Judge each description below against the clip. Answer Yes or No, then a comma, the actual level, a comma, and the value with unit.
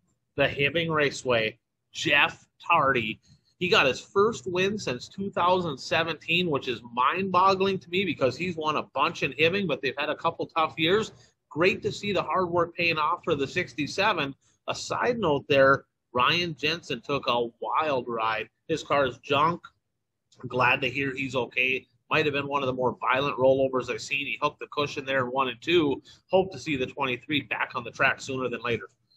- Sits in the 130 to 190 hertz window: Yes, medium, 140 Hz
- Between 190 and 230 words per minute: Yes, average, 195 wpm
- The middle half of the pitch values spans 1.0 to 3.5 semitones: No, average, 4.8 semitones